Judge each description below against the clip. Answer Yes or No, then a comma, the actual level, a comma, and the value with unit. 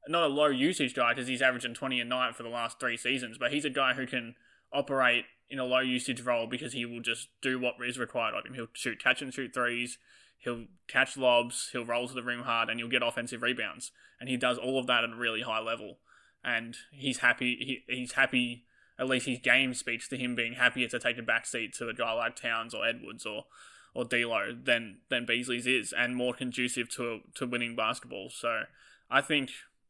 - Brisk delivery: Yes, fast, 225 wpm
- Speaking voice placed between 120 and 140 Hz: Yes, low, 125 Hz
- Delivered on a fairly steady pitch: Yes, narrow, 1.3 semitones